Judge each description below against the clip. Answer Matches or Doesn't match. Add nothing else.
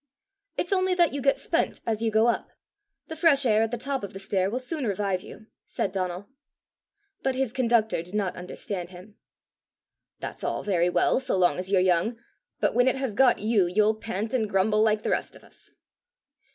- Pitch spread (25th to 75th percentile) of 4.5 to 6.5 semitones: Matches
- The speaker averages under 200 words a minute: Doesn't match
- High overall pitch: Matches